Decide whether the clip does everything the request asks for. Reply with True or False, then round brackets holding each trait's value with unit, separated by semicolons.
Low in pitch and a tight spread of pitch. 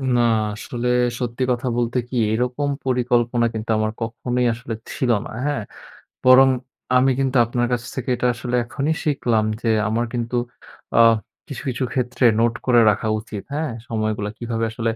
True (120 Hz; 1.9 semitones)